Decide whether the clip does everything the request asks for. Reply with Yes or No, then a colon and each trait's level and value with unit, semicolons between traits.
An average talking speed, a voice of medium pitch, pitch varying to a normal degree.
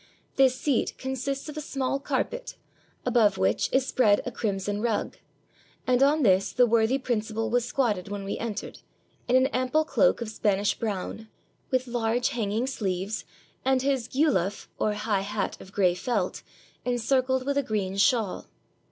No: average, 160 wpm; high, 235 Hz; average, 4.1 semitones